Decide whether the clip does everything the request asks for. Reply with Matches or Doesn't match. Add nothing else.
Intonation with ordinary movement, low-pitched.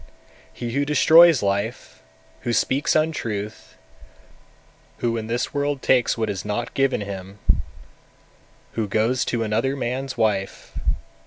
Matches